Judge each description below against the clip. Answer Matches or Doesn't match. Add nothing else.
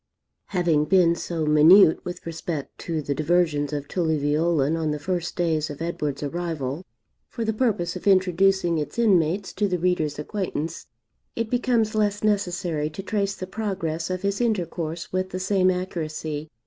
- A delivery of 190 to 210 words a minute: Doesn't match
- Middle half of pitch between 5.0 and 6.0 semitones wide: Doesn't match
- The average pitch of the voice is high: Doesn't match